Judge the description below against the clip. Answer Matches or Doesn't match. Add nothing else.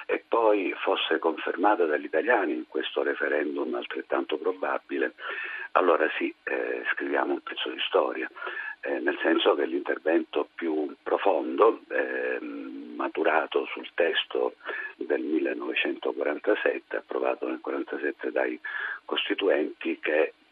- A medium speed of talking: Doesn't match